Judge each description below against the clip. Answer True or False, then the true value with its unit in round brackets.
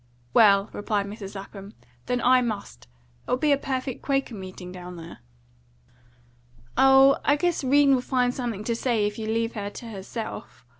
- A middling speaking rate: True (165 wpm)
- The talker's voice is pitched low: False (230 Hz)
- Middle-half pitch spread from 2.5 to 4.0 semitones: False (4.5 semitones)